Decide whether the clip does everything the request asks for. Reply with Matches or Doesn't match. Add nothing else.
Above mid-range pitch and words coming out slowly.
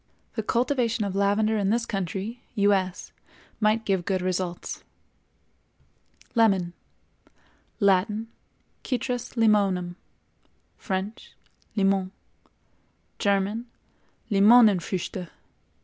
Matches